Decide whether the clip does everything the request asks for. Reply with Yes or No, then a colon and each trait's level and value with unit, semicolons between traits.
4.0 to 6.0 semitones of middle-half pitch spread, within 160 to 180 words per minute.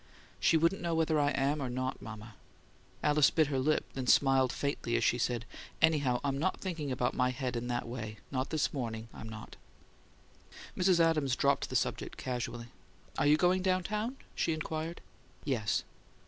Yes: average, 4.6 semitones; average, 175 wpm